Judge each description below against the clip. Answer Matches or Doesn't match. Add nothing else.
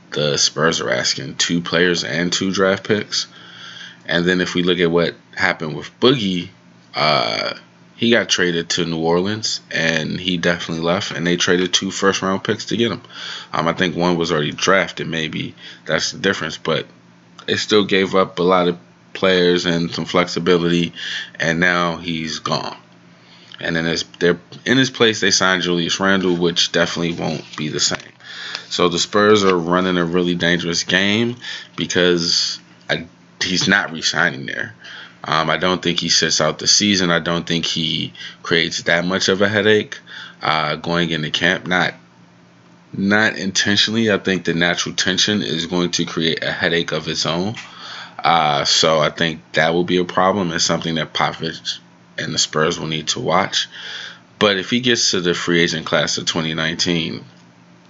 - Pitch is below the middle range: Matches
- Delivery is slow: Doesn't match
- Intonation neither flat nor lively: Doesn't match